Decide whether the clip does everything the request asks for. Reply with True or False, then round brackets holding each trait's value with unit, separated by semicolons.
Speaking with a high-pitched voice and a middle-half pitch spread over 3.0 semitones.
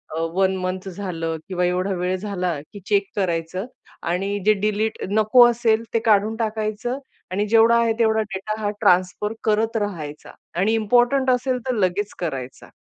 True (205 Hz; 3.4 semitones)